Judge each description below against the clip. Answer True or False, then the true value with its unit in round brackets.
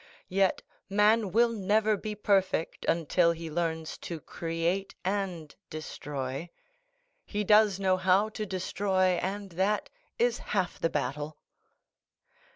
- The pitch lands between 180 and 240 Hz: True (185 Hz)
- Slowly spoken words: True (120 wpm)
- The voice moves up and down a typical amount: True (3.7 semitones)